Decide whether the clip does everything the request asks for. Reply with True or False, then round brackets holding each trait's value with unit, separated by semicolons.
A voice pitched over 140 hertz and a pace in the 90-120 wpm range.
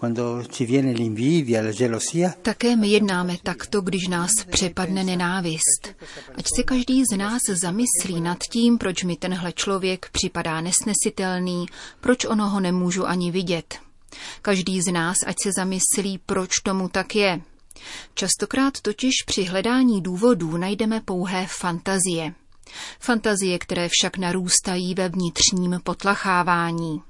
True (185 Hz; 115 wpm)